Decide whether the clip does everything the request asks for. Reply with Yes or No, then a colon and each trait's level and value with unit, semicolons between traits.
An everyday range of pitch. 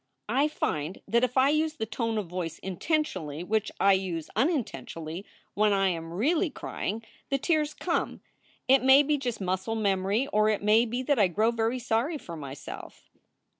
No: wide, 6.1 semitones